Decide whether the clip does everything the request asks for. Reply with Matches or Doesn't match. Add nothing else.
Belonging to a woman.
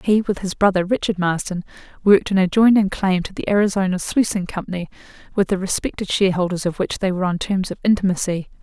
Matches